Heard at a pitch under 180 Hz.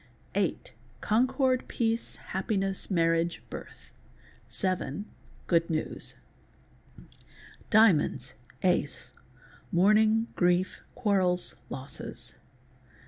No: medium, 185 Hz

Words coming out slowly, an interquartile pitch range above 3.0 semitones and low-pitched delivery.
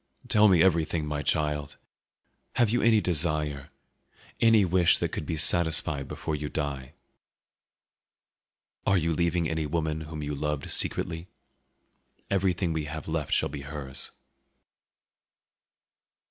No: slow, 125 wpm; average, 2.7 semitones; very low, 80 Hz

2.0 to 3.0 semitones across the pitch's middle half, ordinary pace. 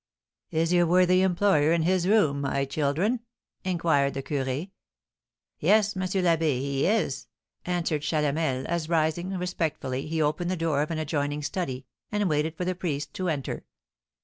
No: average, 3.8 semitones; average, 155 wpm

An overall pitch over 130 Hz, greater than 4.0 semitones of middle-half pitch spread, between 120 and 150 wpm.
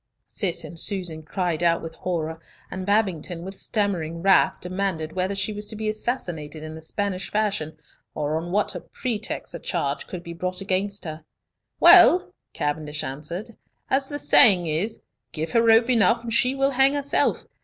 No: medium, 185 Hz; average, 4.9 semitones; average, 170 wpm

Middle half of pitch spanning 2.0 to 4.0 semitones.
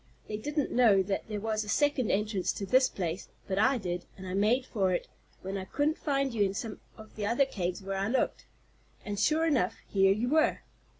No: average, 4.8 semitones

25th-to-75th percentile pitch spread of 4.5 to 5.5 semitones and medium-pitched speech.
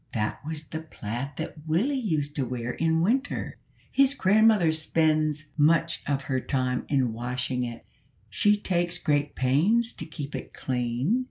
Yes: average, 5.1 semitones; medium, 155 Hz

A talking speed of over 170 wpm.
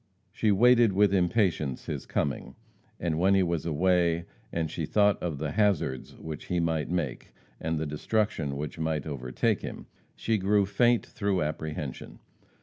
No: average, 155 wpm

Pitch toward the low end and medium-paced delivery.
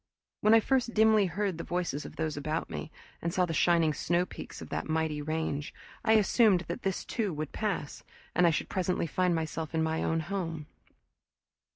No: medium, 170 Hz; average, 190 wpm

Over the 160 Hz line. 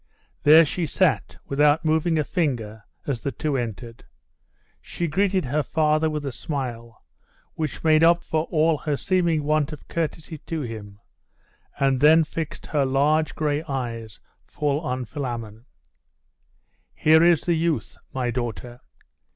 No: medium, 150 Hz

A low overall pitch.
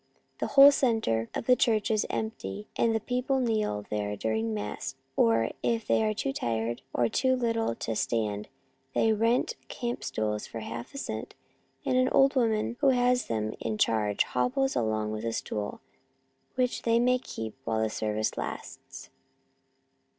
Yes: low, 130 Hz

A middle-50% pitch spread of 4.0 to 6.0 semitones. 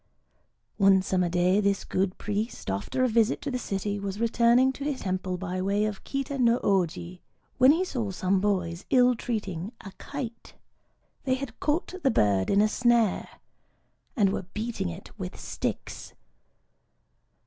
Yes: average, 4.7 semitones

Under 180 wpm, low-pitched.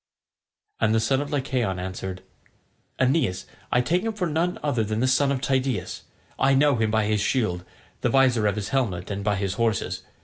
No: average, 195 wpm; low, 120 Hz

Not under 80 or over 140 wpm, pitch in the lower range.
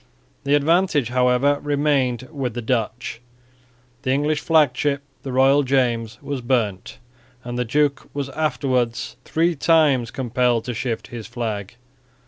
Yes: slow, 135 wpm; low, 130 Hz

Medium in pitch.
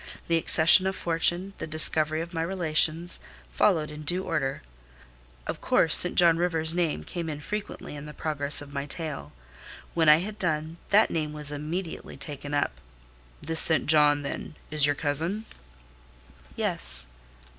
Yes: medium, 155 Hz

